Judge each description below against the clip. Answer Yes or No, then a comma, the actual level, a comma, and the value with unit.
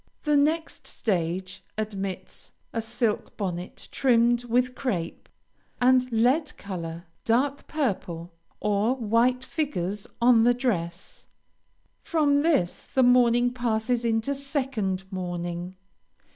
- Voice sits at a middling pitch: No, high, 235 Hz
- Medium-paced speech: No, slow, 105 wpm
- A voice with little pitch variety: No, average, 5.2 semitones